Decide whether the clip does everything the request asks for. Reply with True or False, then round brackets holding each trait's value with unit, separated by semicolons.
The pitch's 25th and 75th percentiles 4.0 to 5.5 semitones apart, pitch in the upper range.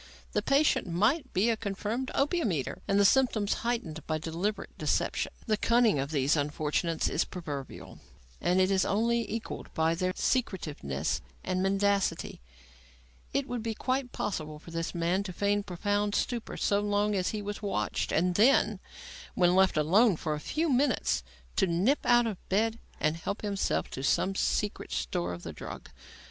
True (5.2 semitones; 200 Hz)